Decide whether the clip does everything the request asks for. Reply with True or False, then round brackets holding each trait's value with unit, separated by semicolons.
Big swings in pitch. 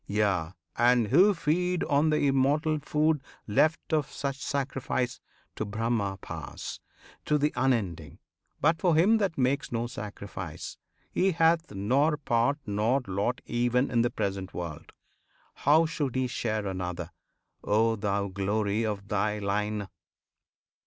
True (6.5 semitones)